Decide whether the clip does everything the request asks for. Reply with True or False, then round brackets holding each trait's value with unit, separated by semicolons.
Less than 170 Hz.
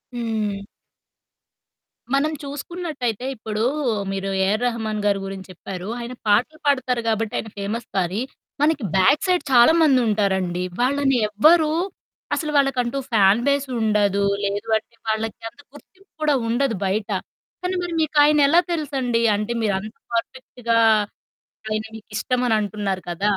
False (230 Hz)